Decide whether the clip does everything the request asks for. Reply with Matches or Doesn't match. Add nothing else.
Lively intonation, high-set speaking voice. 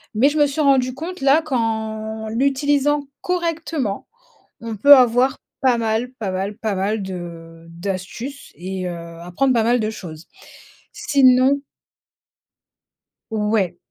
Matches